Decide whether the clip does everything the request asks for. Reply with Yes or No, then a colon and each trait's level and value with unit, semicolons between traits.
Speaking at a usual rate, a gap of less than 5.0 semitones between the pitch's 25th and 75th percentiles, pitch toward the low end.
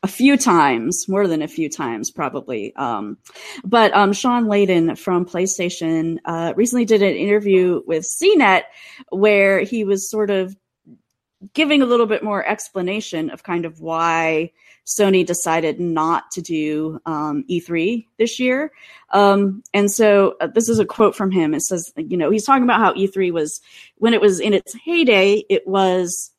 No: average, 170 wpm; average, 4.3 semitones; high, 195 Hz